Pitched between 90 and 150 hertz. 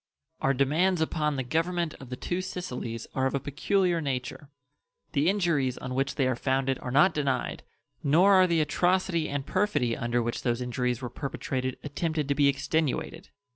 Yes: medium, 140 Hz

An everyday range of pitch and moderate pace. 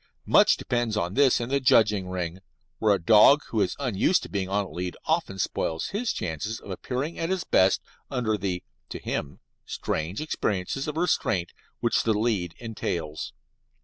No: wide, 5.9 semitones; average, 175 wpm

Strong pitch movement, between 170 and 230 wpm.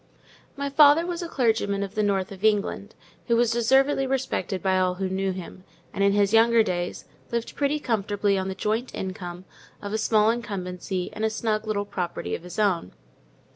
No: average, 3.6 semitones; average, 190 wpm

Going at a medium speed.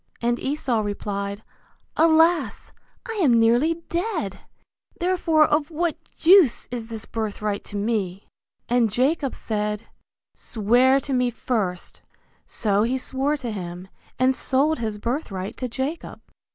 No: slow, 125 wpm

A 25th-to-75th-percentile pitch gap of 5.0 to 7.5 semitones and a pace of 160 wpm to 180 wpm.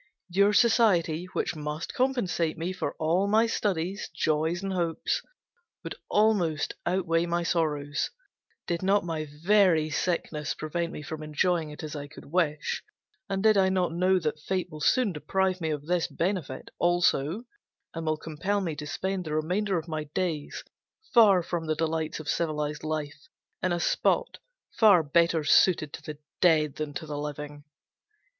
No: average, 3.4 semitones; average, 165 wpm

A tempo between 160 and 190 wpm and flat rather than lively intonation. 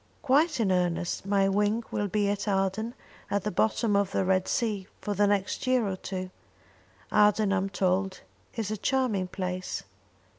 Yes: average, 165 wpm; narrow, 2.3 semitones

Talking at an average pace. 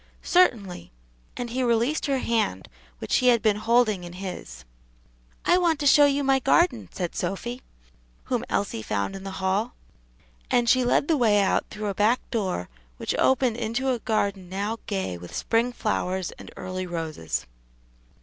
Yes: average, 170 wpm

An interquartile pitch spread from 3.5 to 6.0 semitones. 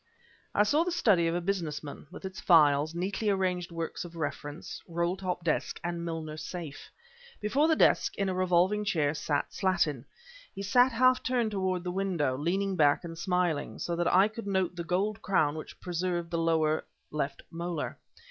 No: average, 3.1 semitones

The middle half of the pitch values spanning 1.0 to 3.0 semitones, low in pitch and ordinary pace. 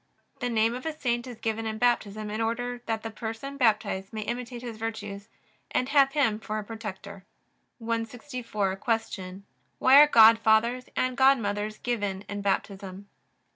No: average, 2.7 semitones; high, 225 Hz; average, 155 wpm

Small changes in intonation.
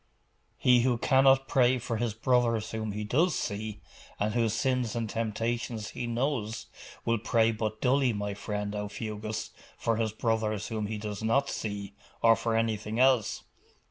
Yes: narrow, 2.2 semitones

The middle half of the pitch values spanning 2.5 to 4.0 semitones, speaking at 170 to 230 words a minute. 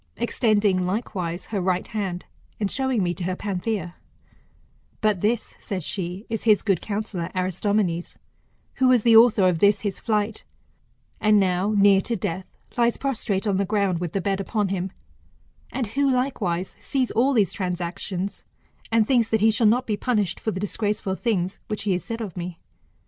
Yes: average, 3.3 semitones; average, 175 wpm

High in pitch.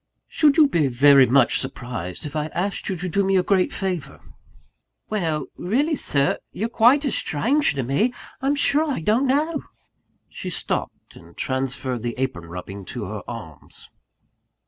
No: medium, 165 Hz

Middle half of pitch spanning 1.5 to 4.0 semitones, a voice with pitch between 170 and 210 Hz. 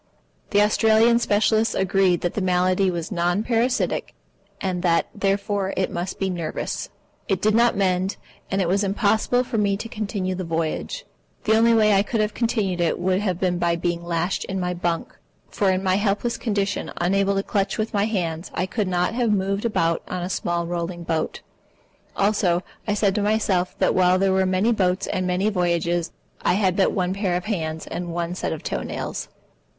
Yes: average, 2.8 semitones; high, 190 Hz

